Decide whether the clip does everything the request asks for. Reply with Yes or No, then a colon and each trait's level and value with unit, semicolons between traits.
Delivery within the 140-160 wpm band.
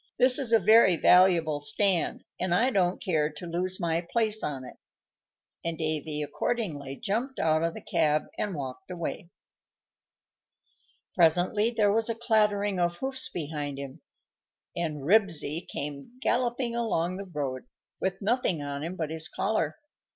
Yes: average, 150 wpm